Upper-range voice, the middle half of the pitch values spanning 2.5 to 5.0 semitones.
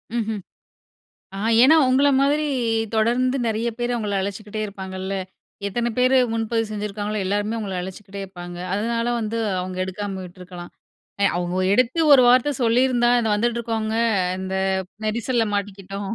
Yes: high, 215 Hz; average, 3.3 semitones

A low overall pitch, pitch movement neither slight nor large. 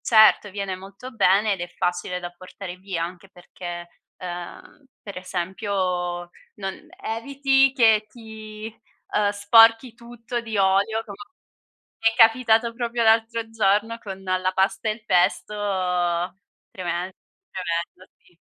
No: high, 205 Hz; average, 3.6 semitones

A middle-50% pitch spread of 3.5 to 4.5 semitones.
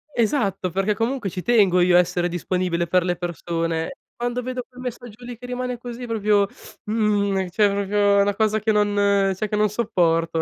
Yes: average, 4.1 semitones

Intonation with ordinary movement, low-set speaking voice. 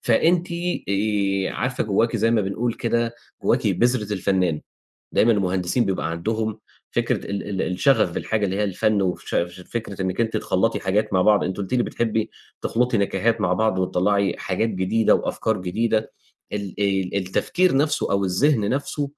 Yes: average, 3.3 semitones; low, 105 Hz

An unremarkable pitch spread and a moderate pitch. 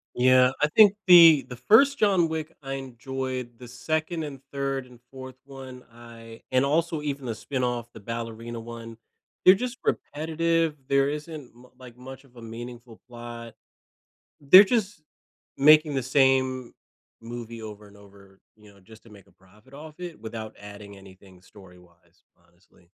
No: average, 4.6 semitones; low, 125 Hz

